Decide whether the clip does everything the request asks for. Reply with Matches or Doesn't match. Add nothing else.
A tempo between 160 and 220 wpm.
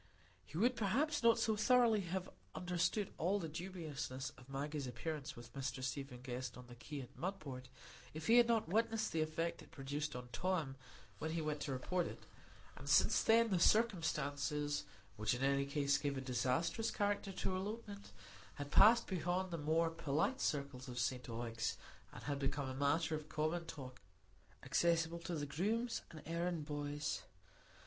Matches